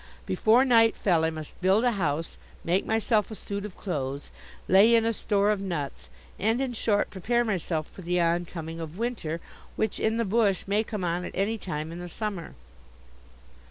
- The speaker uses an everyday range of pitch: Yes, average, 4.8 semitones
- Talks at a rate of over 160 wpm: Yes, average, 190 wpm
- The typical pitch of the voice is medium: No, high, 195 Hz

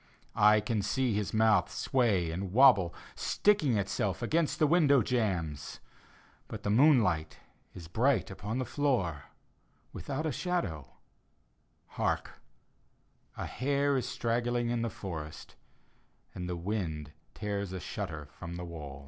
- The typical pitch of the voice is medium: No, low, 105 Hz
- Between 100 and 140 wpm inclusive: Yes, slow, 135 wpm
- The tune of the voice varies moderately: No, wide, 6.6 semitones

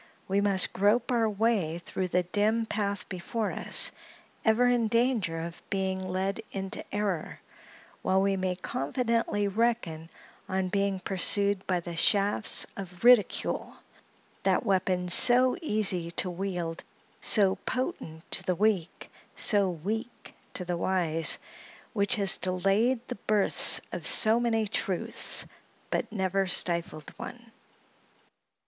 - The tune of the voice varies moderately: Yes, average, 3.3 semitones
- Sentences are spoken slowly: Yes, slow, 125 wpm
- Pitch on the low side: No, high, 195 Hz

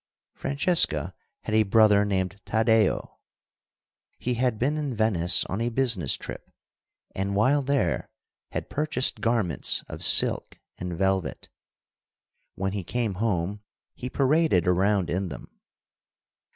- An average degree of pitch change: Yes, average, 5.0 semitones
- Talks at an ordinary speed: No, slow, 125 wpm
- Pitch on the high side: No, low, 105 Hz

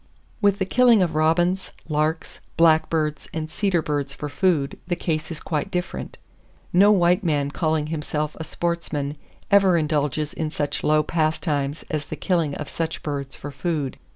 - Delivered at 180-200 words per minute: No, average, 160 wpm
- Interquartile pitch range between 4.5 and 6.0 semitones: No, average, 2.7 semitones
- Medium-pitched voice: Yes, medium, 155 Hz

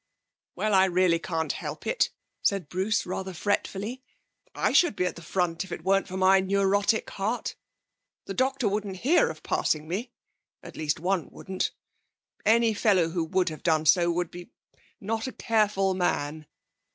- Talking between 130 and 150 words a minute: No, average, 165 wpm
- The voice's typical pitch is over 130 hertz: Yes, high, 190 Hz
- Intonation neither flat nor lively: Yes, average, 3.2 semitones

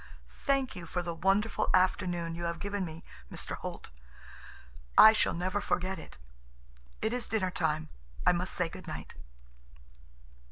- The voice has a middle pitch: Yes, medium, 180 Hz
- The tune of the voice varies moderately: Yes, average, 3.2 semitones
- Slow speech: No, average, 150 wpm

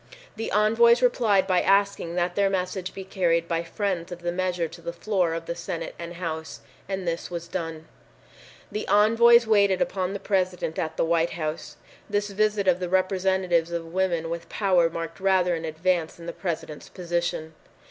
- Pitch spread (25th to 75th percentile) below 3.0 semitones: Yes, narrow, 2.6 semitones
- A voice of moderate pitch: Yes, medium, 180 Hz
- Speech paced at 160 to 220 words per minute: Yes, average, 180 wpm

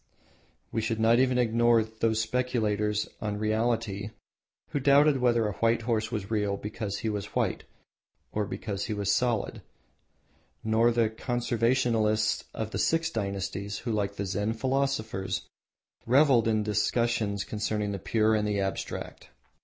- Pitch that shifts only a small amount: Yes, narrow, 2.1 semitones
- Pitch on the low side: Yes, low, 110 Hz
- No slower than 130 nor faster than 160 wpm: Yes, average, 145 wpm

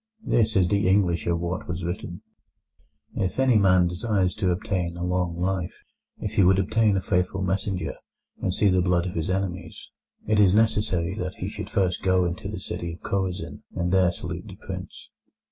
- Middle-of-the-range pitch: No, very low, 95 Hz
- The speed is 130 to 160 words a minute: No, average, 190 wpm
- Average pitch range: No, narrow, 1.9 semitones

